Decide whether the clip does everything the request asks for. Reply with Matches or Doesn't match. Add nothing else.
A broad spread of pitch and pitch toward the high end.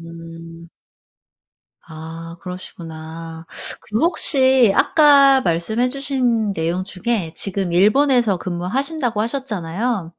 Matches